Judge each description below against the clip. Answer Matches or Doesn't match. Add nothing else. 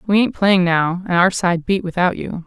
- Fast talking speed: Matches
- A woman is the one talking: Matches